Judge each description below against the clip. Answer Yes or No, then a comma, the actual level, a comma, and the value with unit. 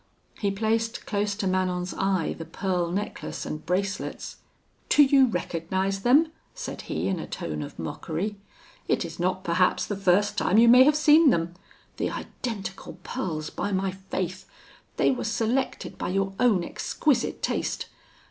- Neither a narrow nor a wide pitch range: Yes, average, 3.9 semitones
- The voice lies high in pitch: Yes, high, 195 Hz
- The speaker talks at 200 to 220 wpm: No, average, 155 wpm